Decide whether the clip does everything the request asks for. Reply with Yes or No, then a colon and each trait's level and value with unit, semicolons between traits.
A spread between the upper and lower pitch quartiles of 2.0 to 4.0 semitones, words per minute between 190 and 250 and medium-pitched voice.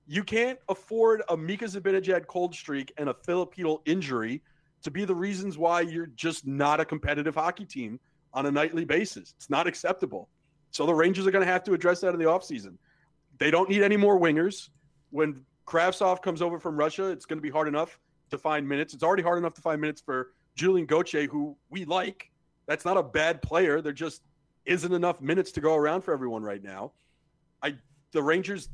Yes: average, 3.5 semitones; average, 200 wpm; medium, 160 Hz